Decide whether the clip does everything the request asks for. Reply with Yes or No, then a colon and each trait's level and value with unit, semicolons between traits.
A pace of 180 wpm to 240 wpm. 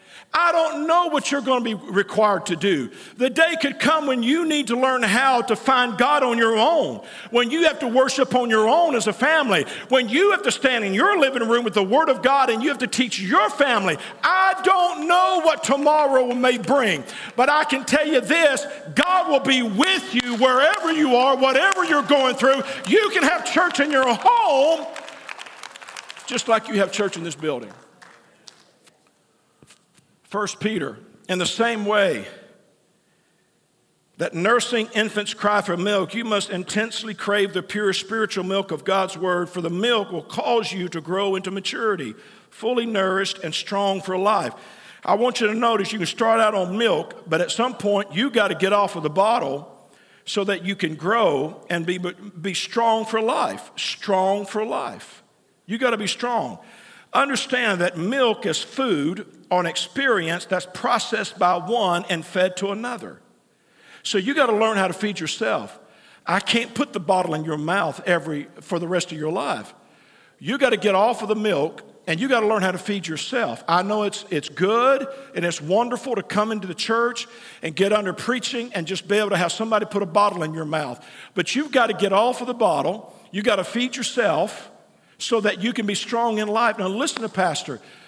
Yes: average, 195 wpm